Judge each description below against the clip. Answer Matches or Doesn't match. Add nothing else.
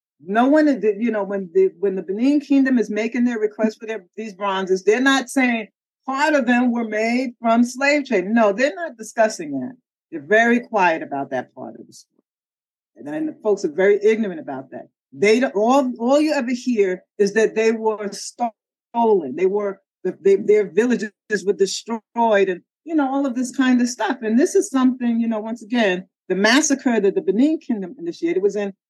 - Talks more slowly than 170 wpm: Doesn't match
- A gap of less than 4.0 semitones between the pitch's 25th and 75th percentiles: Doesn't match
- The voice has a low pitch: Doesn't match